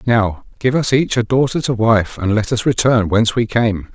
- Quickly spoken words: Yes, fast, 230 wpm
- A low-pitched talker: Yes, low, 115 Hz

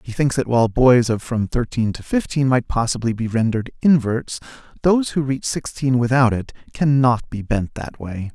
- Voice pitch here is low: Yes, low, 125 Hz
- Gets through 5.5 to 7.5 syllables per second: No, 5.0 syllables/s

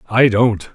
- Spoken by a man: Yes, male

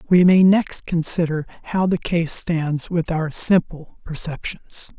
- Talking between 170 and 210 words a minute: No, average, 145 wpm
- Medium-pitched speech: Yes, medium, 165 Hz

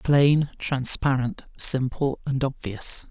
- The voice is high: No, low, 135 Hz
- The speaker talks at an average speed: No, slow, 95 wpm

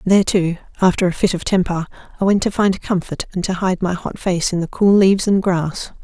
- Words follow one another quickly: Yes, fast, 240 wpm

